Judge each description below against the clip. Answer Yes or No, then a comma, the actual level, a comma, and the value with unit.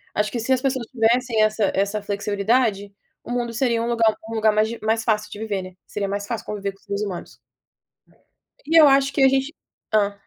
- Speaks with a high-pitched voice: Yes, high, 220 Hz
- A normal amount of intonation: Yes, average, 3.1 semitones